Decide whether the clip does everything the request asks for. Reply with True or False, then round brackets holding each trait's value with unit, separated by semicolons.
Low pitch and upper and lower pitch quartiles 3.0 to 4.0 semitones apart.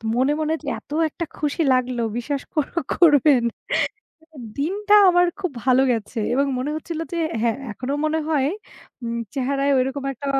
False (280 Hz; 3.5 semitones)